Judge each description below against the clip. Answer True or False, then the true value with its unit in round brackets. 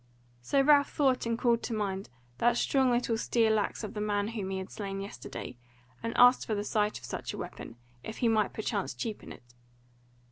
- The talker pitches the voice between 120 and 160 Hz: False (220 Hz)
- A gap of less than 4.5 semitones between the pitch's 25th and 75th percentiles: True (2.8 semitones)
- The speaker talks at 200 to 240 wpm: True (205 wpm)